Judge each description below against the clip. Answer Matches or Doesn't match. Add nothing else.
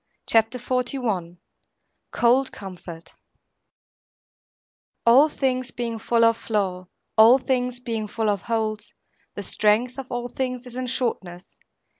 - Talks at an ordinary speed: Doesn't match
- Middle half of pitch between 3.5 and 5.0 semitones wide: Doesn't match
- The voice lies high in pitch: Matches